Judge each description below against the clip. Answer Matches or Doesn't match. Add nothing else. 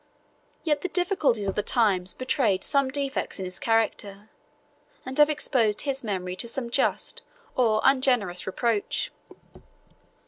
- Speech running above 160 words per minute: Doesn't match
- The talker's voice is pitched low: Doesn't match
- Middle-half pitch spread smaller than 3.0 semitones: Doesn't match